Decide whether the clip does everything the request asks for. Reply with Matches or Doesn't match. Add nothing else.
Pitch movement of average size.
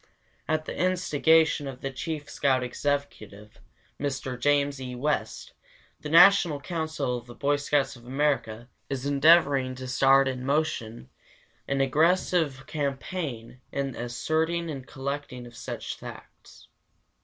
Matches